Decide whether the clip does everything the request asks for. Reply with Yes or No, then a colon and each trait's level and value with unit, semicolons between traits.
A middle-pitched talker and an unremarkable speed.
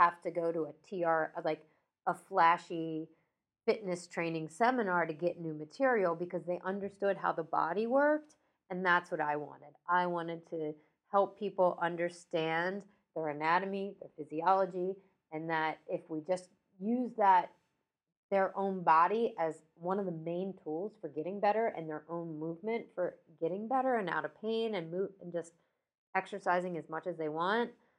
Yes: medium, 175 Hz; average, 165 wpm